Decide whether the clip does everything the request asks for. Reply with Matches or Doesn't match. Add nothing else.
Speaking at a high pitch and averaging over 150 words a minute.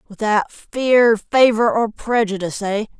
Doesn't match